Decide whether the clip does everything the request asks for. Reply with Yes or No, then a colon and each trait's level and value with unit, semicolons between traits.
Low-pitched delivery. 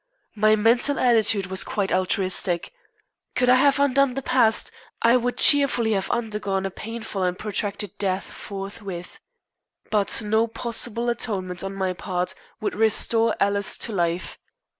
No: high, 215 Hz